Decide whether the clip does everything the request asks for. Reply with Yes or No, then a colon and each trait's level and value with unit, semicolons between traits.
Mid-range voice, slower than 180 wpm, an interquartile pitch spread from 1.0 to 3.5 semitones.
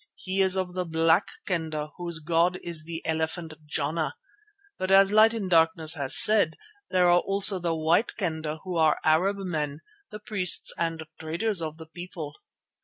Yes: medium, 170 Hz; average, 170 wpm; average, 2.8 semitones